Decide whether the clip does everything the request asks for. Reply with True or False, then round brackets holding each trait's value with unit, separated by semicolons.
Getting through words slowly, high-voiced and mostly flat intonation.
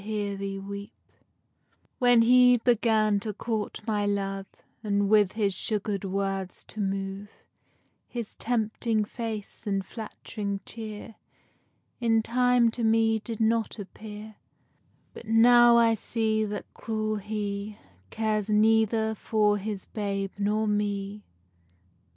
True (115 wpm; 215 Hz; 1.8 semitones)